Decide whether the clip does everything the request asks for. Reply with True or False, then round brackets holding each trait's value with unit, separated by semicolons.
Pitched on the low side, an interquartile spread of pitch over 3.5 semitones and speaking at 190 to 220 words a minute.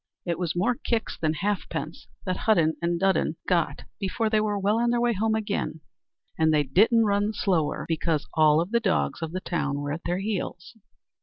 False (185 Hz; 5.0 semitones; 200 wpm)